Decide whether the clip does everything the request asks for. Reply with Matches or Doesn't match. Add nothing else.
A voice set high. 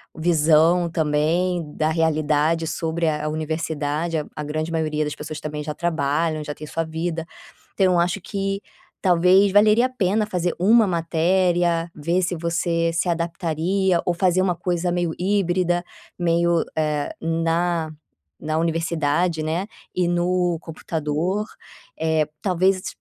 Doesn't match